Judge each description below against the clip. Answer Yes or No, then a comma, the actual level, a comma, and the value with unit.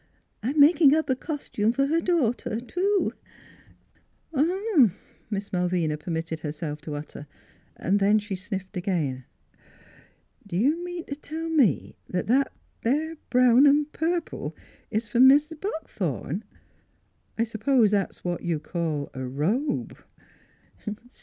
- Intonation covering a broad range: Yes, wide, 8.8 semitones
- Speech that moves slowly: Yes, slow, 125 wpm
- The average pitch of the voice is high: Yes, high, 230 Hz